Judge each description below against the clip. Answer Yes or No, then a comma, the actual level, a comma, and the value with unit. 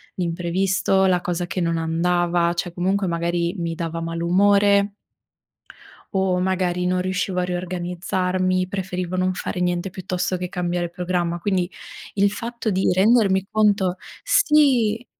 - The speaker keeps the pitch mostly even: Yes, narrow, 1.7 semitones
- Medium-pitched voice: Yes, medium, 180 Hz